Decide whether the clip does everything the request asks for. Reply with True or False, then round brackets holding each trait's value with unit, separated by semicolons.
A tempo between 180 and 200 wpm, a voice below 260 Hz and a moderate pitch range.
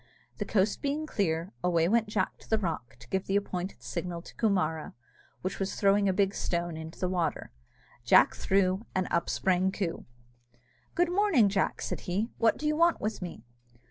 True (185 wpm; 190 Hz; 3.7 semitones)